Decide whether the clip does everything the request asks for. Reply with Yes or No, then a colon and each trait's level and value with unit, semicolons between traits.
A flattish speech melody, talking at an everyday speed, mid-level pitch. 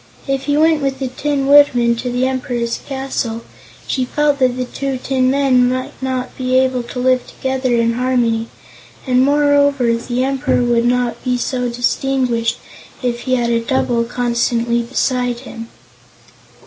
No: narrow, 1.8 semitones; average, 160 wpm; very high, 255 Hz